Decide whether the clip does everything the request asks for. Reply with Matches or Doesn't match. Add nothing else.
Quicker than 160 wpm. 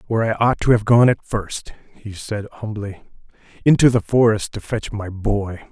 Matches